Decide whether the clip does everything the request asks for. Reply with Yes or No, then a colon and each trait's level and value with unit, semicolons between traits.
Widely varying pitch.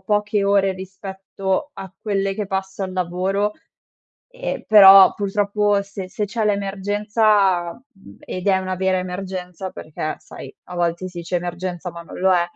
No: narrow, 1.9 semitones